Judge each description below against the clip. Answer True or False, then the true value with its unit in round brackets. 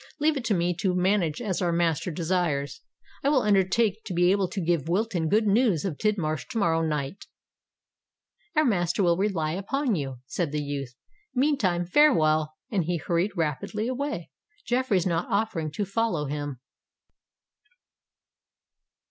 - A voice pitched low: False (180 Hz)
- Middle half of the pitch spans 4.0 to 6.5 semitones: True (4.9 semitones)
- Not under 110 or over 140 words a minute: False (150 wpm)